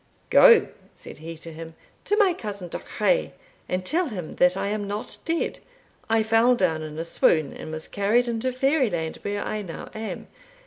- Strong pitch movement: Yes, wide, 6.8 semitones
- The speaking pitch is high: Yes, high, 205 Hz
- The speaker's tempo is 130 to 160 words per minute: No, average, 180 wpm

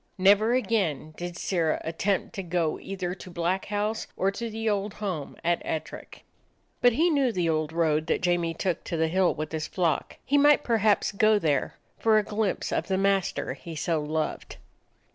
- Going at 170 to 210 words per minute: Yes, average, 185 wpm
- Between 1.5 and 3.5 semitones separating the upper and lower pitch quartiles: No, average, 4.5 semitones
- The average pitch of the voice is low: No, medium, 185 Hz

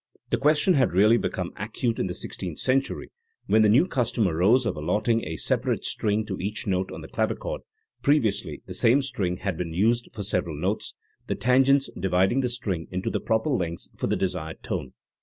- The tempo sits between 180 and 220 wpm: Yes, average, 195 wpm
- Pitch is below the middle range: Yes, low, 105 Hz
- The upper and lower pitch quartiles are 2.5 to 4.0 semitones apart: No, wide, 5.4 semitones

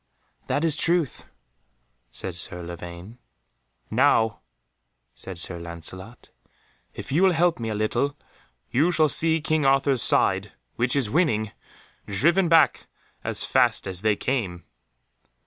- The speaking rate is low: Yes, slow, 130 wpm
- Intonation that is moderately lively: No, wide, 8.8 semitones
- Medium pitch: No, low, 125 Hz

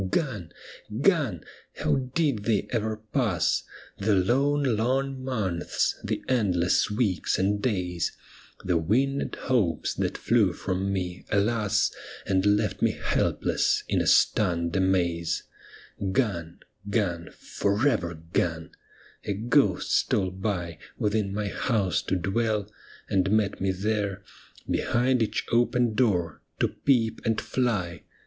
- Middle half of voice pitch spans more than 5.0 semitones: No, average, 4.4 semitones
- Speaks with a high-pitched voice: No, low, 105 Hz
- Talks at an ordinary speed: No, slow, 130 wpm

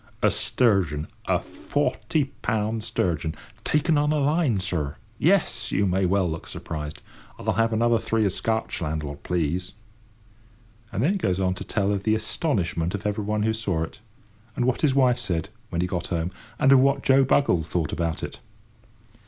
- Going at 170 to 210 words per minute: Yes, average, 175 wpm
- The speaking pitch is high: No, low, 105 Hz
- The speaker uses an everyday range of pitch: No, wide, 6.0 semitones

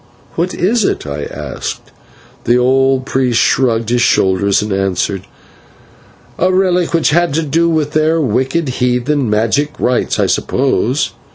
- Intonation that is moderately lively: No, wide, 6.2 semitones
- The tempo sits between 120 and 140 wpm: No, average, 150 wpm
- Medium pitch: No, low, 130 Hz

